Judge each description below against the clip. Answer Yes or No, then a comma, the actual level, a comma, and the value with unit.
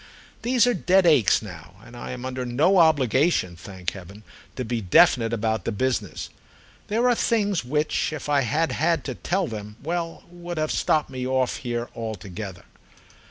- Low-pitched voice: Yes, low, 130 Hz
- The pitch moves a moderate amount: No, wide, 7.0 semitones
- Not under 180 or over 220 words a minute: No, average, 165 wpm